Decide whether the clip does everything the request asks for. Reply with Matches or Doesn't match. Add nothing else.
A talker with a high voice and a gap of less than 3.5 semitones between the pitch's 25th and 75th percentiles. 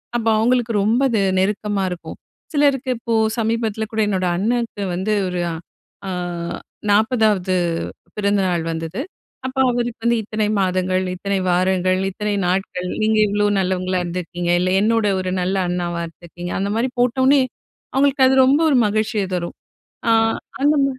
Doesn't match